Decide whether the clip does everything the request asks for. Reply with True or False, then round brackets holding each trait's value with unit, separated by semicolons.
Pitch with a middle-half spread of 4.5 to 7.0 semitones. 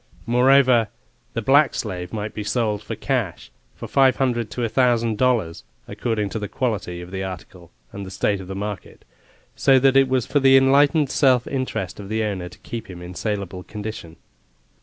True (5.0 semitones)